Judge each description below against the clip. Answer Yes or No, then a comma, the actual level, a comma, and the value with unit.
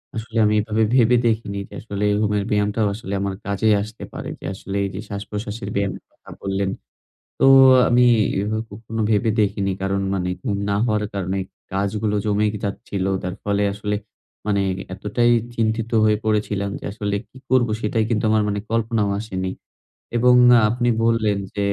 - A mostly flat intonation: Yes, narrow, 1.8 semitones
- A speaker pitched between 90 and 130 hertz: Yes, low, 105 Hz